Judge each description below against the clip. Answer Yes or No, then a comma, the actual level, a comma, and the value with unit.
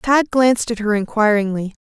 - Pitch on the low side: No, high, 225 Hz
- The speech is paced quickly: No, average, 165 wpm